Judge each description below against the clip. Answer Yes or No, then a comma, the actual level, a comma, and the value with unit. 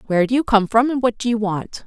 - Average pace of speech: No, fast, 320 wpm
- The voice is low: No, high, 225 Hz